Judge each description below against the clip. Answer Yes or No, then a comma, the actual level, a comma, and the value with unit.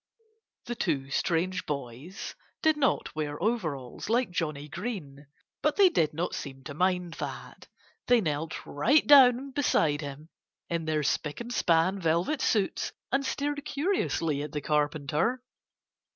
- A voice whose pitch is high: No, medium, 170 Hz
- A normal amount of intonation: No, wide, 8.6 semitones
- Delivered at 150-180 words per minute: No, average, 140 wpm